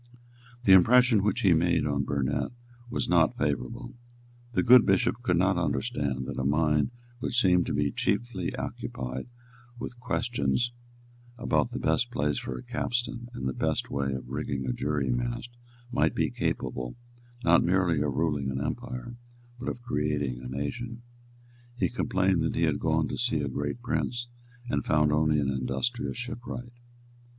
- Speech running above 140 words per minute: Yes, average, 165 wpm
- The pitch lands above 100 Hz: No, very low, 80 Hz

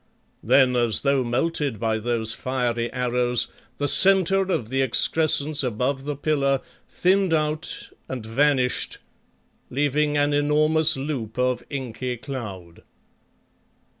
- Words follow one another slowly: Yes, slow, 115 wpm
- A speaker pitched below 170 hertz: Yes, low, 135 Hz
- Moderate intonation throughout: Yes, average, 3.4 semitones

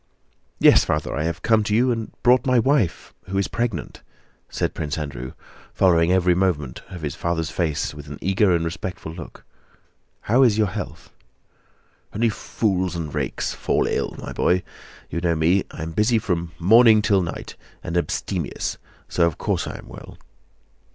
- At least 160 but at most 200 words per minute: Yes, average, 170 wpm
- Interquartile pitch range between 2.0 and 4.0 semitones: No, average, 4.4 semitones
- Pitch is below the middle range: Yes, very low, 90 Hz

